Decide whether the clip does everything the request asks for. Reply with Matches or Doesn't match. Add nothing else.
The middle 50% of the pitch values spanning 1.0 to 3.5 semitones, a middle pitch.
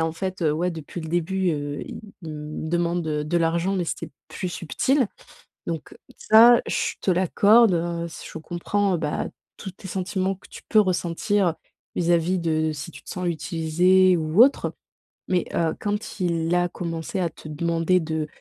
Matches